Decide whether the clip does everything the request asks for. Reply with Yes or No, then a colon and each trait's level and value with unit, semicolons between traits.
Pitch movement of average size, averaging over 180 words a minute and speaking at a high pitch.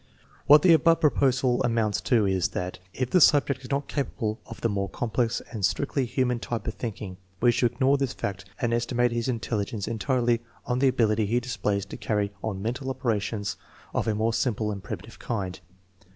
No: average, 3.6 semitones; average, 190 wpm; low, 115 Hz